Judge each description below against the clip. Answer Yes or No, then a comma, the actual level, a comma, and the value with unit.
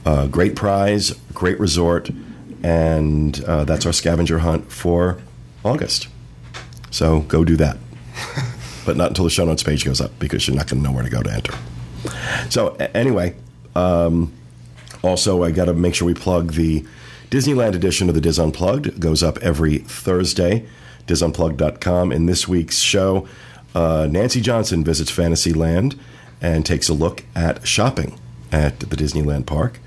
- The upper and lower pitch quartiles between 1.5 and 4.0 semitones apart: Yes, average, 2.9 semitones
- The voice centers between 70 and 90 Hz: Yes, very low, 85 Hz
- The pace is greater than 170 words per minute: No, average, 165 wpm